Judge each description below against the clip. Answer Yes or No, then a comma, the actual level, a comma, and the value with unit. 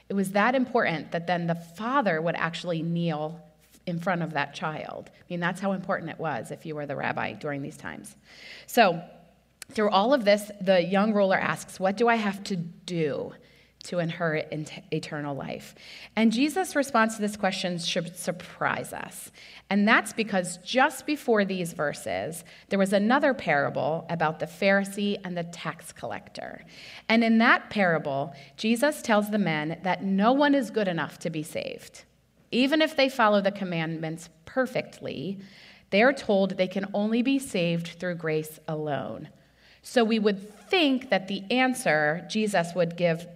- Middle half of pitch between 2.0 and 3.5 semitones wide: No, average, 4.7 semitones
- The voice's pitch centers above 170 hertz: Yes, high, 190 Hz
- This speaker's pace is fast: No, average, 170 wpm